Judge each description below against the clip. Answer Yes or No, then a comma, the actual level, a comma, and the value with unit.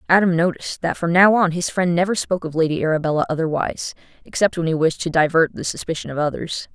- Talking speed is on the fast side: Yes, fast, 215 wpm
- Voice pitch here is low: No, medium, 170 Hz